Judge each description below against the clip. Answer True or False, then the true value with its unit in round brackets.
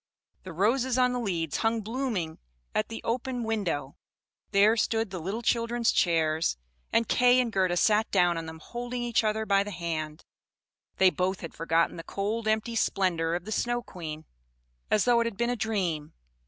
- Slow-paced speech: False (185 wpm)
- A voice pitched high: True (210 Hz)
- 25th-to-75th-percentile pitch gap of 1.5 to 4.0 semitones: False (5.4 semitones)